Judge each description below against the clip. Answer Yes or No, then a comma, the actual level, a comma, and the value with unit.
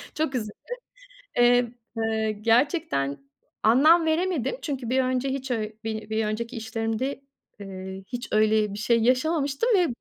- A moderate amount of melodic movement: Yes, average, 4.0 semitones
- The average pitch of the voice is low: No, high, 235 Hz